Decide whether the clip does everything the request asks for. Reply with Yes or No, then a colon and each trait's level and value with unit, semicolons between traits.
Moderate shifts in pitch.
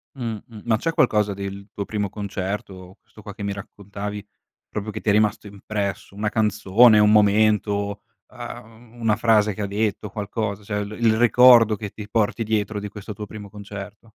No: narrow, 1.3 semitones